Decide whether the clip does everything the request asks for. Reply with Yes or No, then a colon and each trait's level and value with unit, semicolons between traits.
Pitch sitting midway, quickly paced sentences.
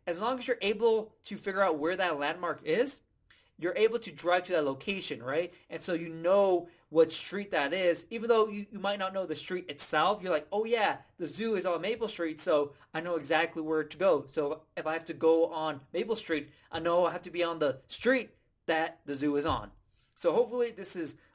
Yes: medium, 175 Hz; fast, 230 wpm